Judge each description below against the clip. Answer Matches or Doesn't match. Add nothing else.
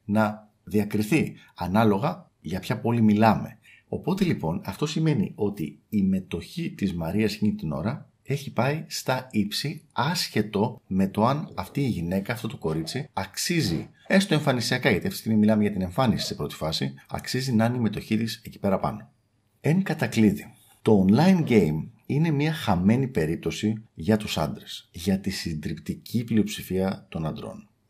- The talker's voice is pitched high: Doesn't match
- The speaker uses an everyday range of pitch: Doesn't match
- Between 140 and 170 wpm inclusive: Matches